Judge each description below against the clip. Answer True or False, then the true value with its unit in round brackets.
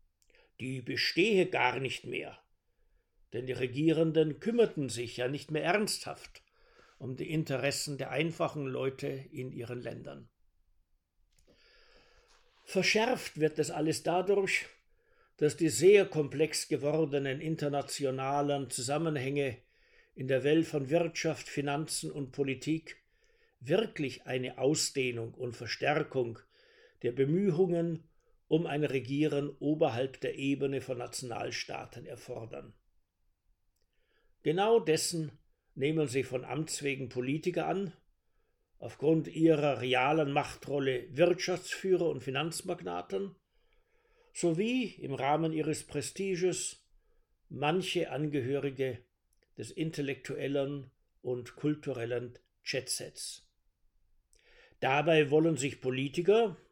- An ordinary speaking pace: False (95 wpm)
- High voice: False (145 Hz)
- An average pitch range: True (4.4 semitones)